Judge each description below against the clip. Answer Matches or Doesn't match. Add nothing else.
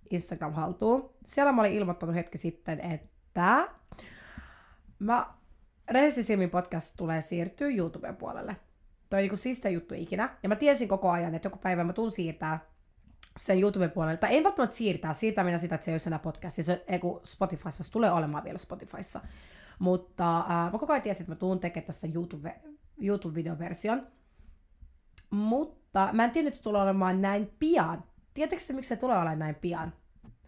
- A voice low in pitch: Doesn't match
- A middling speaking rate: Doesn't match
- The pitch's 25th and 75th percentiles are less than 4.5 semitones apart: Doesn't match